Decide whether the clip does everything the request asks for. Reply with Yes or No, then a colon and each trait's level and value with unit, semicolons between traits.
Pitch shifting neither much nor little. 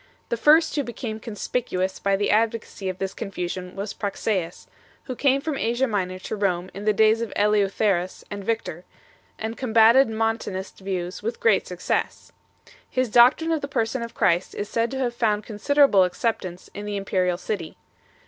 Yes: average, 3.5 semitones